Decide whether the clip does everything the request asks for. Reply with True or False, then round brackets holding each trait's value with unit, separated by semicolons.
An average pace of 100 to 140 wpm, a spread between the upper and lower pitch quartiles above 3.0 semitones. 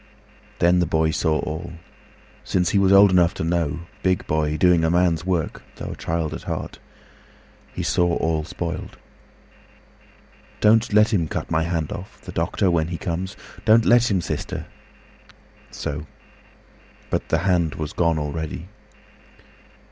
False (135 wpm; 2.5 semitones)